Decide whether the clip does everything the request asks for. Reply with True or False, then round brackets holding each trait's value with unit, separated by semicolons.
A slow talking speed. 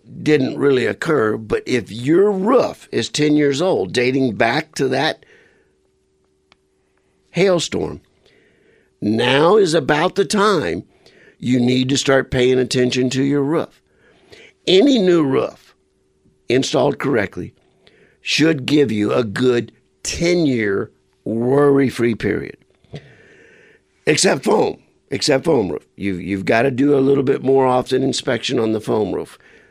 True (125 wpm)